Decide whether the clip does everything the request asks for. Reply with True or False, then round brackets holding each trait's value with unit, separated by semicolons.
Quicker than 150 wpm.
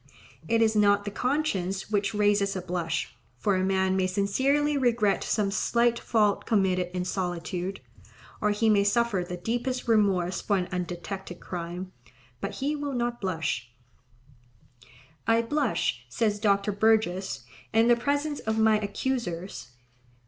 False (140 wpm)